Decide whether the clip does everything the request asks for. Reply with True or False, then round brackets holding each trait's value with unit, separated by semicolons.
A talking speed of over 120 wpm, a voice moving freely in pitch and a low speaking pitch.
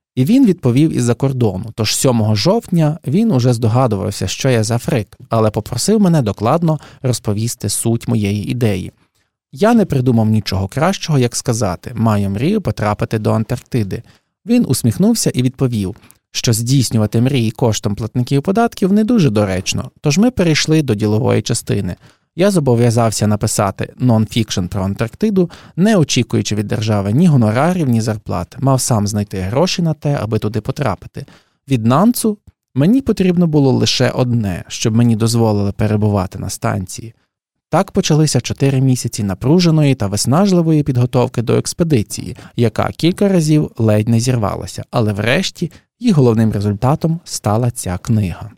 True (140 wpm; 5.9 semitones; 120 Hz)